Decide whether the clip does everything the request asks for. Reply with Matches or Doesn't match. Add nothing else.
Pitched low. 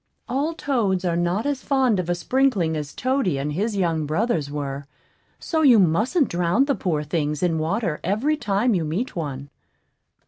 Doesn't match